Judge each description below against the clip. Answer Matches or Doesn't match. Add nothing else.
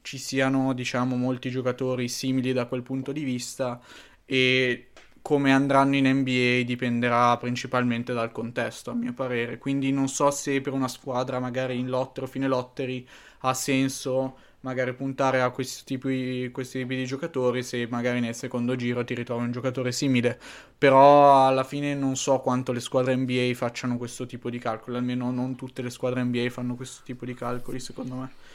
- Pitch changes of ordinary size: Doesn't match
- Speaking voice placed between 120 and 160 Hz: Matches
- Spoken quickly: Matches